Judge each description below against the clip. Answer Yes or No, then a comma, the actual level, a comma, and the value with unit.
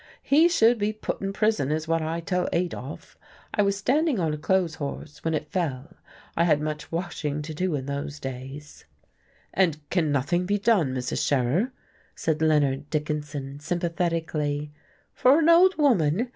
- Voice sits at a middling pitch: Yes, medium, 160 Hz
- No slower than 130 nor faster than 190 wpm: Yes, average, 165 wpm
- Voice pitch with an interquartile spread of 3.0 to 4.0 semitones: No, average, 4.8 semitones